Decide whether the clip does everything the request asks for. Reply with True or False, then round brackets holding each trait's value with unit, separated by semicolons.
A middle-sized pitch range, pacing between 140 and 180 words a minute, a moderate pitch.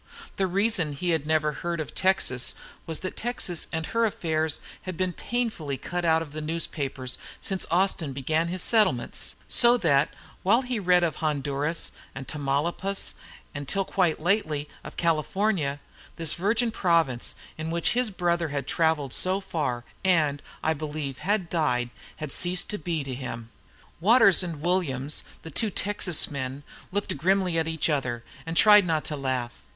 True (4.4 semitones; 165 wpm; 165 Hz)